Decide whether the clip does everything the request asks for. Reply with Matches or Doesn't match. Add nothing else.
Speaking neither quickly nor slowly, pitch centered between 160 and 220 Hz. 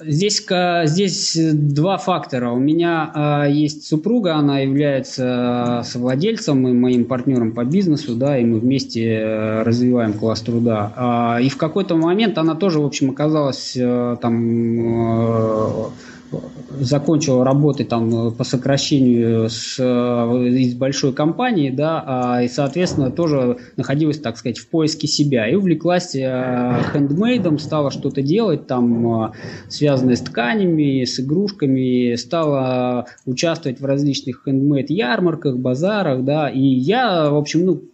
Doesn't match